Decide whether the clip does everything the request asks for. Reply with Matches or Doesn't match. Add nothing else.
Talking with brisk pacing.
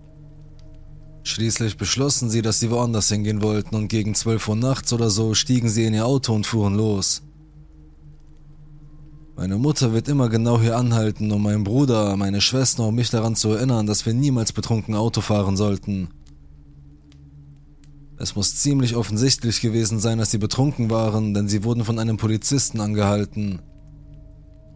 Doesn't match